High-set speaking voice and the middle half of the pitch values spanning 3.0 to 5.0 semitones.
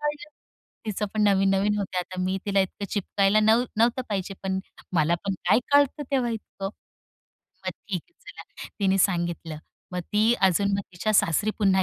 No: high, 200 Hz; narrow, 2.4 semitones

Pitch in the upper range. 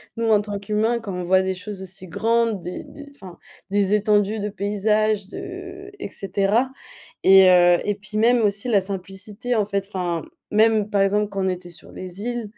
Yes: high, 205 Hz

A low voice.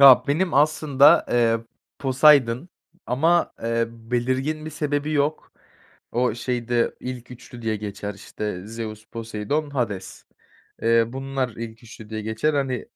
Yes: low, 125 Hz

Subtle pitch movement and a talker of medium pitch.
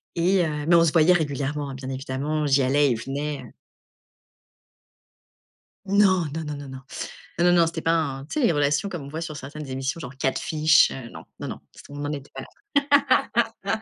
No: average, 3.3 semitones; medium, 150 Hz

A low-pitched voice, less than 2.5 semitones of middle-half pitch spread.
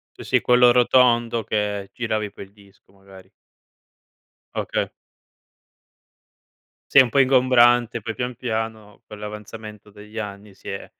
No: low, 110 Hz; average, 2.8 semitones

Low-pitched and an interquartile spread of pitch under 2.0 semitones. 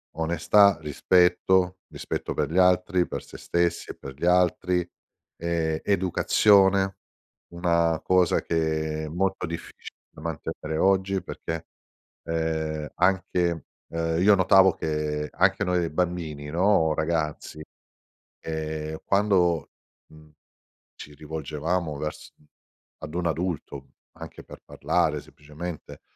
No: very low, 85 Hz; average, 2.7 semitones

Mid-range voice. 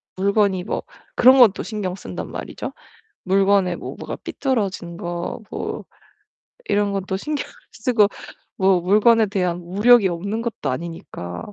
No: high, 195 Hz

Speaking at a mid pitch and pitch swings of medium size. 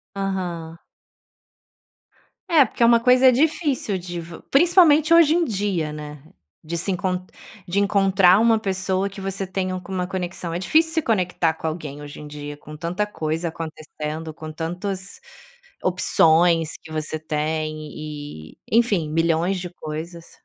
Yes: medium, 180 Hz; average, 4.2 semitones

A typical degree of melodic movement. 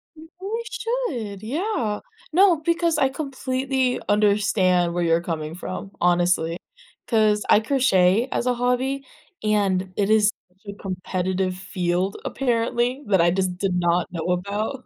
No: wide, 6.1 semitones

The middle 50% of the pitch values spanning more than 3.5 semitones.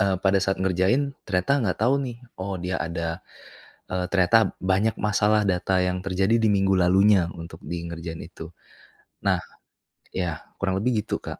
No: narrow, 2.6 semitones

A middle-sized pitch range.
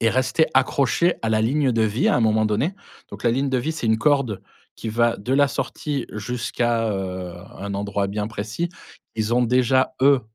Yes: average, 3.6 semitones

